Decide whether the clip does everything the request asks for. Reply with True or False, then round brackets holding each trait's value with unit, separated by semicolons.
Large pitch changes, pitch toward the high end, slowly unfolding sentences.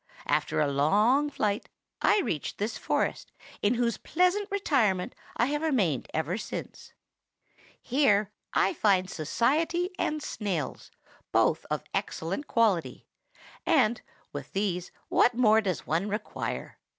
True (7.6 semitones; 215 Hz; 125 wpm)